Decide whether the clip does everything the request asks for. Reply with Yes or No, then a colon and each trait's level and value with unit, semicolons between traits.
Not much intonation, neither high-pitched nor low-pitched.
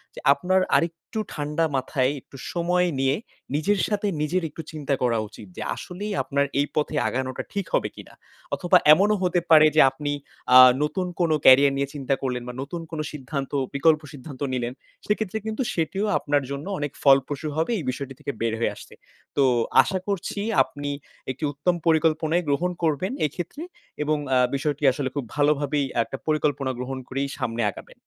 No: average, 3.7 semitones; medium, 150 Hz